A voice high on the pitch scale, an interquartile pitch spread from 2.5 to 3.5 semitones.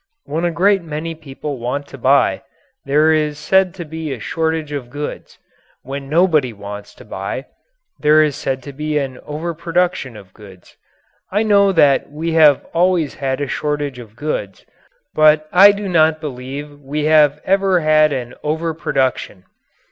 No: medium, 150 Hz; average, 3.2 semitones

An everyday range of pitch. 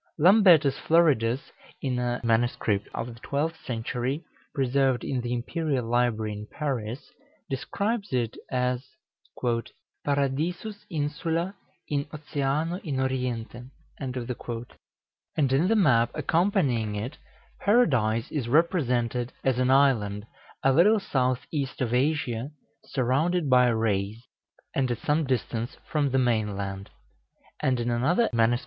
Yes: average, 4.1 semitones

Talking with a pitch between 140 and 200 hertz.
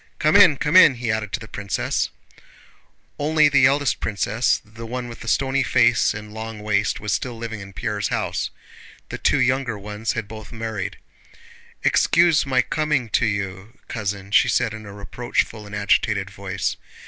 No: low, 110 Hz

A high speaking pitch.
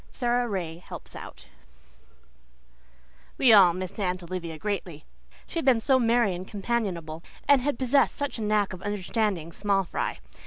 Yes: high, 205 Hz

